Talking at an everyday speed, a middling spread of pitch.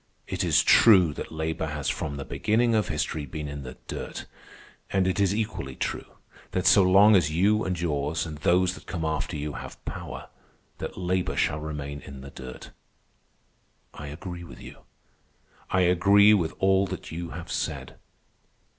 Yes: average, 170 wpm; average, 4.2 semitones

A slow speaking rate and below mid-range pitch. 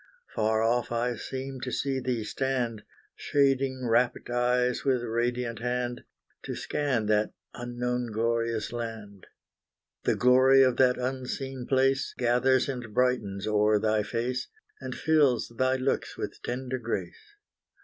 Yes: slow, 130 wpm; low, 125 Hz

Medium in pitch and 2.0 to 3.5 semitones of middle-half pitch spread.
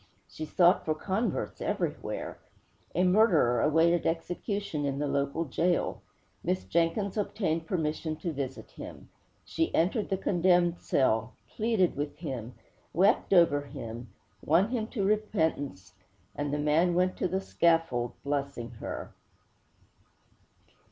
No: medium, 165 Hz; average, 4.6 semitones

